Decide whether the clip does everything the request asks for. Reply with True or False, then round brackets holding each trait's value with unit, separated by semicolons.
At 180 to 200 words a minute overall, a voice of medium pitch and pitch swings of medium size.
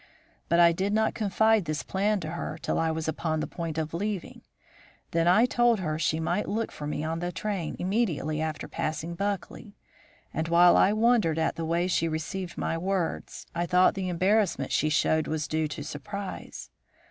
True (190 wpm; 170 Hz; 4.0 semitones)